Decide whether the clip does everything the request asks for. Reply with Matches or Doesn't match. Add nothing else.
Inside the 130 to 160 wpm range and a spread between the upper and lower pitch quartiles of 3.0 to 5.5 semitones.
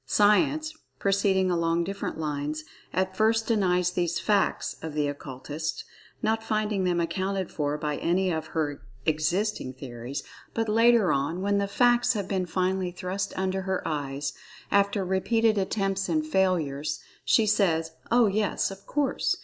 Matches